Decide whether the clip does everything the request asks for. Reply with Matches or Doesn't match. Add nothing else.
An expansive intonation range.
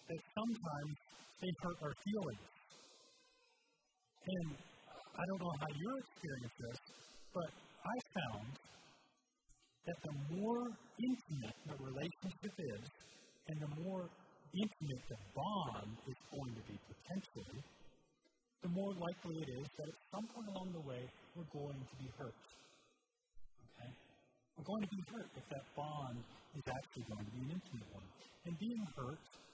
Matches